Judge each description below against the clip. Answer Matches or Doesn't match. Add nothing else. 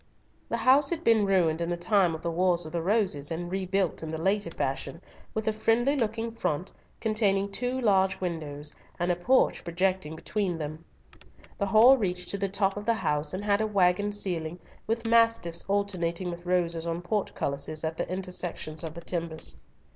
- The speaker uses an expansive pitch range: Doesn't match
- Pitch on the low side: Doesn't match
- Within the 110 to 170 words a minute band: Doesn't match